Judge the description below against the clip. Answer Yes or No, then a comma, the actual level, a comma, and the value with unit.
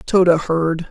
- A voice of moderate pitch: Yes, medium, 170 Hz